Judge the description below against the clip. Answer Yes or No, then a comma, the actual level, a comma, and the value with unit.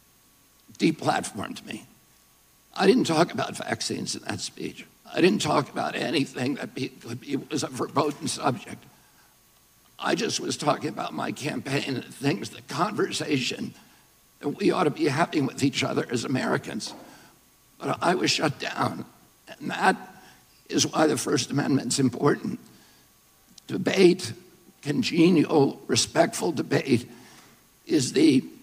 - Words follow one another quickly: No, average, 140 wpm